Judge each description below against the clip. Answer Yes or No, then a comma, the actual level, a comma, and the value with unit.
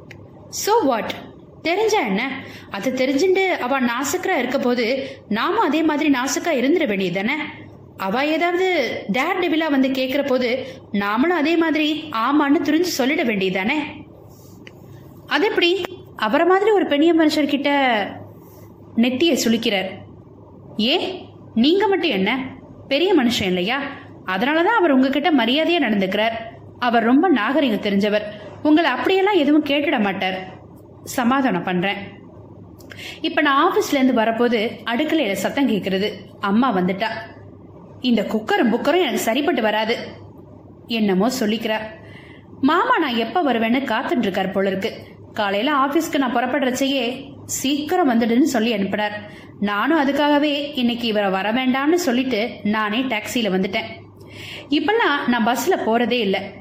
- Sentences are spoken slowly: Yes, slow, 70 wpm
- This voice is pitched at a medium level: No, very high, 265 Hz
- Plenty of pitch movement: Yes, wide, 5.8 semitones